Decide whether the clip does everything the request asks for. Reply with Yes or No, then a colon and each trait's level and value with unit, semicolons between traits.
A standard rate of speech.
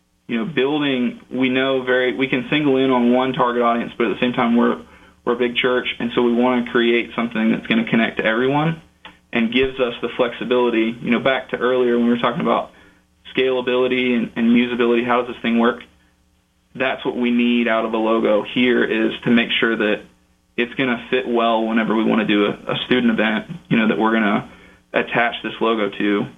No: fast, 225 wpm